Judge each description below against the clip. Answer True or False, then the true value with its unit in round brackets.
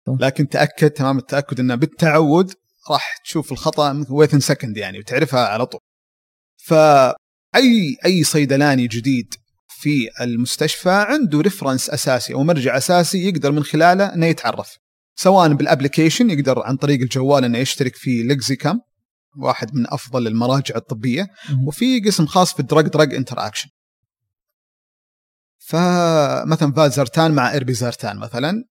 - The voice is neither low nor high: True (145 Hz)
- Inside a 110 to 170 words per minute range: True (125 wpm)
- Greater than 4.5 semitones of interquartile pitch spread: False (3.9 semitones)